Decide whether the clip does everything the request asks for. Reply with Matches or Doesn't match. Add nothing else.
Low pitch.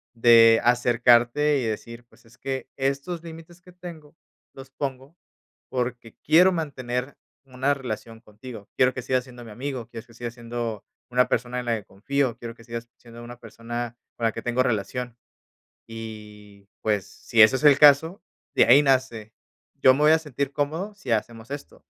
Matches